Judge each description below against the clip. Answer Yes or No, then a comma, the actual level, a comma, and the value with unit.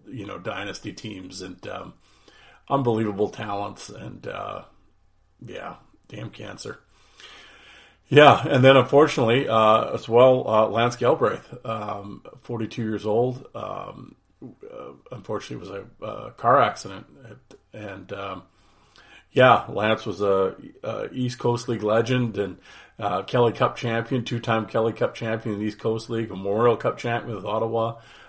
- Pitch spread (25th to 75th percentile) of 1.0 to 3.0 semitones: Yes, narrow, 2.4 semitones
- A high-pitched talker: No, low, 115 Hz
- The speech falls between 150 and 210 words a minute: No, average, 140 wpm